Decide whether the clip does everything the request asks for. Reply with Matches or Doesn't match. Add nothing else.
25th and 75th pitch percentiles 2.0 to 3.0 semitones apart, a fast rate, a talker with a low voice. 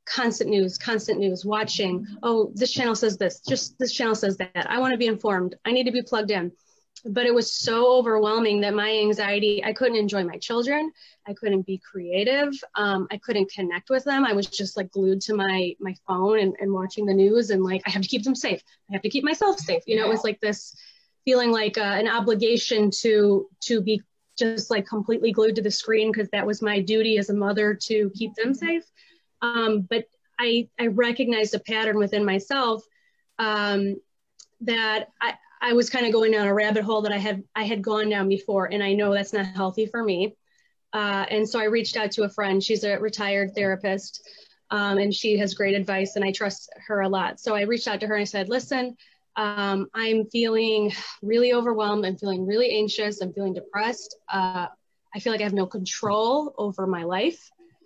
Doesn't match